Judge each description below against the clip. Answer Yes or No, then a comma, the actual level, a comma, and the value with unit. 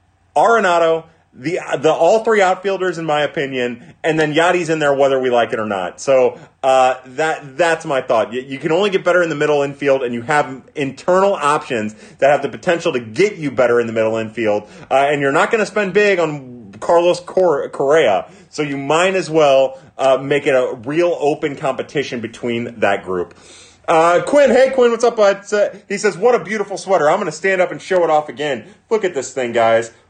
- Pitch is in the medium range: Yes, medium, 150 Hz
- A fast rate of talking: Yes, fast, 215 wpm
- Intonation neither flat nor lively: No, wide, 5.8 semitones